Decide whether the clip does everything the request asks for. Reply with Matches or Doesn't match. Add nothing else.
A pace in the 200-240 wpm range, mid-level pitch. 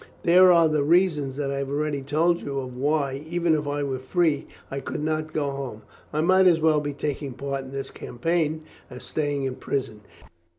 Matches